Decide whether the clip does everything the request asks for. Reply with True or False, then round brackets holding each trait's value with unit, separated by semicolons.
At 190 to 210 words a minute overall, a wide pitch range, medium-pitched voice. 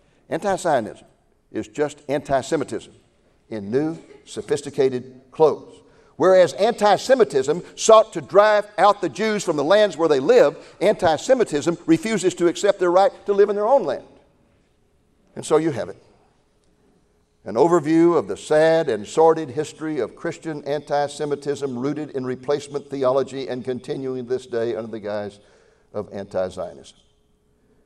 False (150 wpm; 6.5 semitones; 155 Hz)